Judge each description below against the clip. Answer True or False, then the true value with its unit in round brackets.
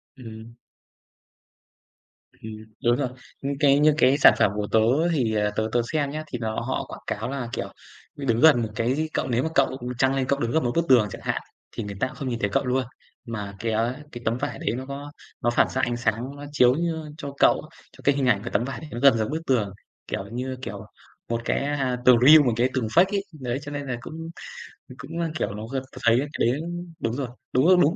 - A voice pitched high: False (130 Hz)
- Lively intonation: False (3.5 semitones)